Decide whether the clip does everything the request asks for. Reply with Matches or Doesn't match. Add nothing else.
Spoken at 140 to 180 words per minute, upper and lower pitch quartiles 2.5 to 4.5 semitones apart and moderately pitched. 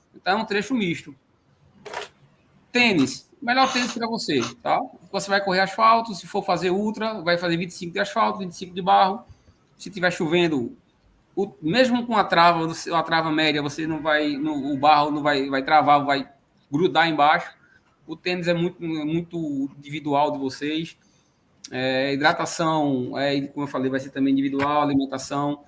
Doesn't match